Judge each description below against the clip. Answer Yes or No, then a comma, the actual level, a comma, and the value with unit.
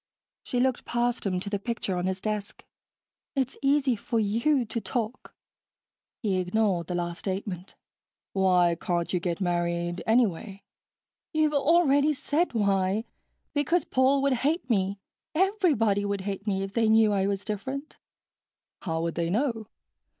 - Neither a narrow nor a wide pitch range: No, wide, 5.7 semitones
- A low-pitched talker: No, high, 210 Hz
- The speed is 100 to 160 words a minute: Yes, average, 150 wpm